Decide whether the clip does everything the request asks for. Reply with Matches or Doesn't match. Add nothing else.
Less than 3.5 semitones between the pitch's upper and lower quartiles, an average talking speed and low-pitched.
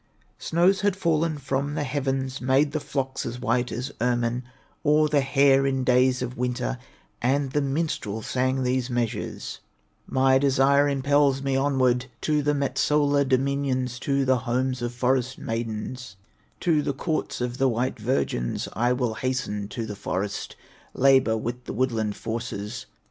Matches